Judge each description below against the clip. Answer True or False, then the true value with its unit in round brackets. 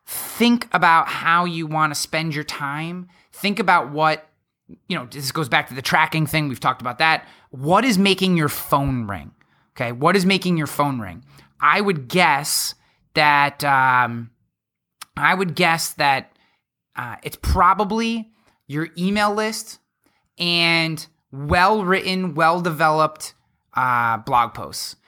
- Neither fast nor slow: True (145 wpm)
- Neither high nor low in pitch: True (155 Hz)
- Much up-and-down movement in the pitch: False (4.2 semitones)